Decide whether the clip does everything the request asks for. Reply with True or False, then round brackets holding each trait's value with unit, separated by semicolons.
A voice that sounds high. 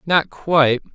False (150 Hz)